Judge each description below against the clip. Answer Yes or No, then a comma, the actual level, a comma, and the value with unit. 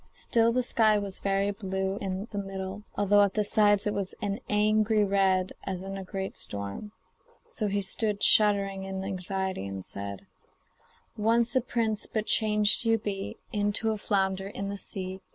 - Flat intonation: Yes, narrow, 1.7 semitones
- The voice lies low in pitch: No, high, 200 Hz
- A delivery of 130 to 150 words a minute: No, average, 170 wpm